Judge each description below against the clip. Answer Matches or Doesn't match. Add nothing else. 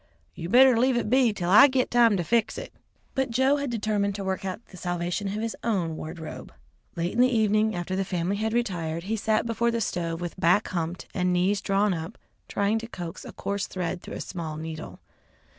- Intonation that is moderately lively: Matches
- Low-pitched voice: Doesn't match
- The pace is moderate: Doesn't match